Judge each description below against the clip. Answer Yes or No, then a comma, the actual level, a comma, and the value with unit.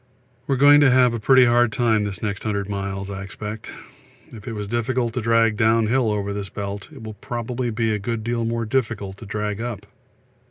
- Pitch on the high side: No, low, 110 Hz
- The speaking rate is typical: No, fast, 210 wpm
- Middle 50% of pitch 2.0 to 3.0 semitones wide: Yes, narrow, 2.6 semitones